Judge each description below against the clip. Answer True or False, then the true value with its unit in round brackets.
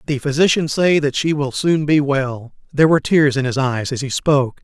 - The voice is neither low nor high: True (145 Hz)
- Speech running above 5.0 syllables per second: True (5.4 syllables/s)